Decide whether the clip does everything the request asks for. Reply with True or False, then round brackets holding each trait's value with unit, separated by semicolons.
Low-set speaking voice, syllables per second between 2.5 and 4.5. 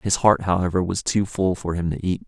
False (90 Hz; 5.4 syllables/s)